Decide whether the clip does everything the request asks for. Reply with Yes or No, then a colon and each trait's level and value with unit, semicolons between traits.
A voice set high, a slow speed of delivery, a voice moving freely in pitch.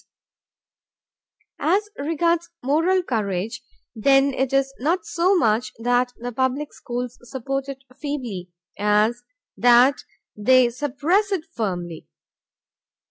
No: very high, 260 Hz; slow, 105 wpm; average, 4.2 semitones